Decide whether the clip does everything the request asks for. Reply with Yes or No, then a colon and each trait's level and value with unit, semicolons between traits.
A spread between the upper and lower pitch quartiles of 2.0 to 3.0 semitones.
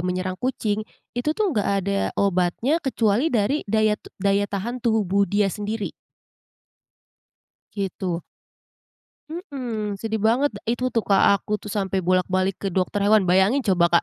No: average, 3.5 semitones